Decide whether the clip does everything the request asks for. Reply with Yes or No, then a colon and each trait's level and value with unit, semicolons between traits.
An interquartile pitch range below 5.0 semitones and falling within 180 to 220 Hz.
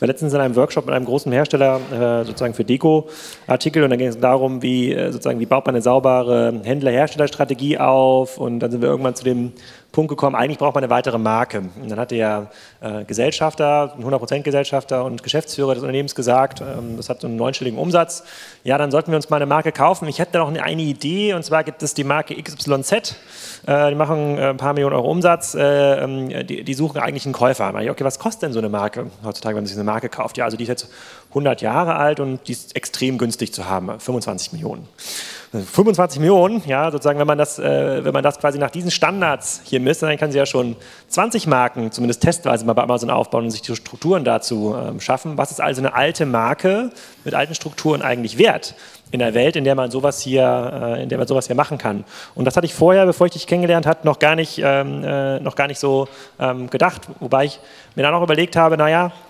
No: average, 3.8 semitones; low, 135 Hz